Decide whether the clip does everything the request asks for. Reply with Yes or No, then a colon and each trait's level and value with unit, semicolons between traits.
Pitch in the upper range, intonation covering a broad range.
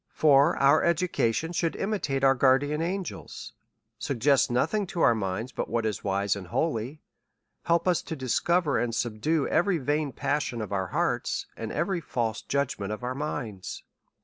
No: medium, 140 Hz; wide, 6.1 semitones